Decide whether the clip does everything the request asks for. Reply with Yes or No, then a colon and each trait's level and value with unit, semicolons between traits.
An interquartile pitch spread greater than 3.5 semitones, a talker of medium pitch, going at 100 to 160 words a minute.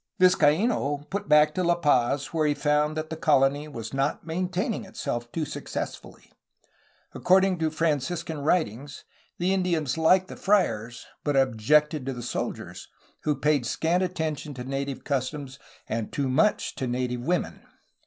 Yes: average, 4.1 semitones; medium, 150 Hz; average, 155 wpm